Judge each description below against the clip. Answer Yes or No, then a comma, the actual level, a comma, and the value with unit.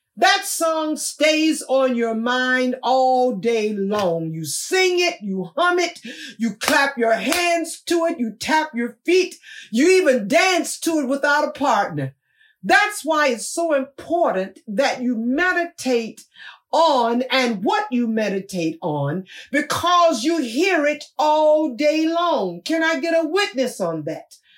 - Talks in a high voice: Yes, very high, 285 Hz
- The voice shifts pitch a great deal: Yes, wide, 6.1 semitones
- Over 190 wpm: No, average, 150 wpm